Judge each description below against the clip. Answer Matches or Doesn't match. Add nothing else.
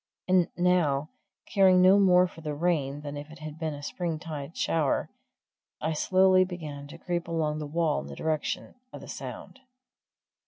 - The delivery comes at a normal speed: Matches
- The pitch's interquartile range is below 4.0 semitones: Matches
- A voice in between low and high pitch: Matches